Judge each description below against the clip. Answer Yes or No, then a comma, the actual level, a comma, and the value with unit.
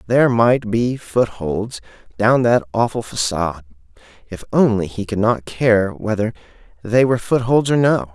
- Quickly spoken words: No, average, 145 wpm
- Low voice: Yes, low, 110 Hz